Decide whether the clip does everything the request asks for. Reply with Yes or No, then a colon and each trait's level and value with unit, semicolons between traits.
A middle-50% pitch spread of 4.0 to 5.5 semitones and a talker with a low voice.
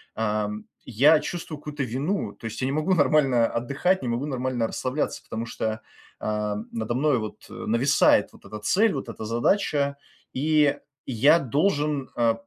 Yes: average, 4.7 semitones; low, 130 Hz